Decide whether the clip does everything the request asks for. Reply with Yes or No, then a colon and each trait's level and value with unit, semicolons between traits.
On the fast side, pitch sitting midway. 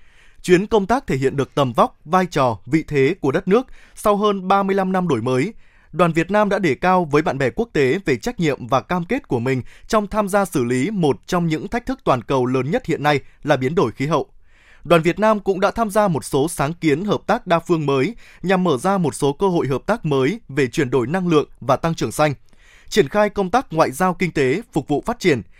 Yes: fast, 255 wpm; medium, 170 Hz